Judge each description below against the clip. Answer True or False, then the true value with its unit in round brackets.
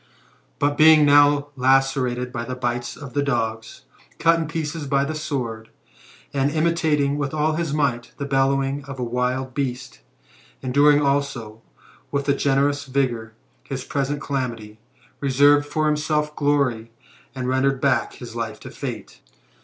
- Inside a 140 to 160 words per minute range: True (150 wpm)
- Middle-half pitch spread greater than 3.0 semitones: False (2.4 semitones)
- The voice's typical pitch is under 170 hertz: True (140 Hz)